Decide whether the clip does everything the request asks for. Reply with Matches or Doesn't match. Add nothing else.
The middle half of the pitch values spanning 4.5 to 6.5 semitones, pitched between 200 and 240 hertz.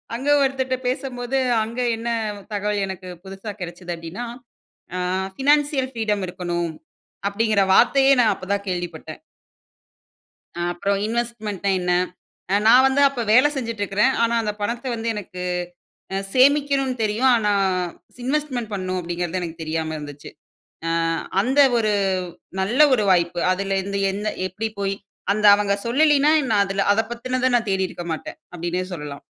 Matches